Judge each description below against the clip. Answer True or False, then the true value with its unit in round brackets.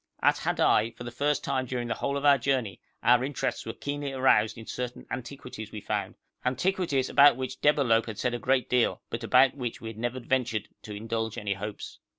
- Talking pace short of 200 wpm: False (205 wpm)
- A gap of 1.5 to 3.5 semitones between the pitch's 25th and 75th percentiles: True (3.0 semitones)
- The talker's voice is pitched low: True (125 Hz)